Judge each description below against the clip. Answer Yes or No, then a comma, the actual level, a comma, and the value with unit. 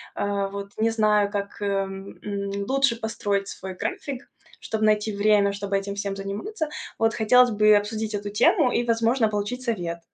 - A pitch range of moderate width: No, narrow, 2.2 semitones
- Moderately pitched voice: No, high, 210 Hz